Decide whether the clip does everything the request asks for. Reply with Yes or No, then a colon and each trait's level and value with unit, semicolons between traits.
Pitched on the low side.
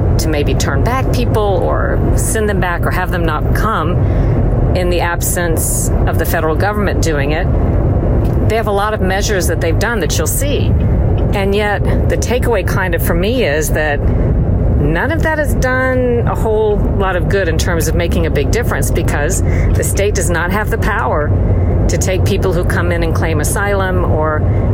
Yes: low, 100 Hz